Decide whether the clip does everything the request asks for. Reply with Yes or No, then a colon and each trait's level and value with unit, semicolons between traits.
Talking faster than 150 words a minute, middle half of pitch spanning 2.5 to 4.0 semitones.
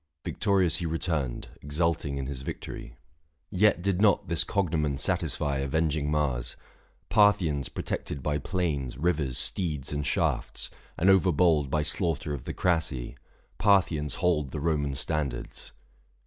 No: average, 140 wpm; average, 3.7 semitones